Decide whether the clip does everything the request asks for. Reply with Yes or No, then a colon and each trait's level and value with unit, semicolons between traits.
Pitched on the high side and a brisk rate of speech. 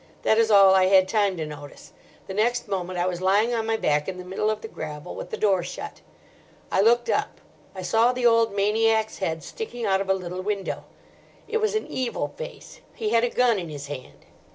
Yes: high, 200 Hz; fast, 225 wpm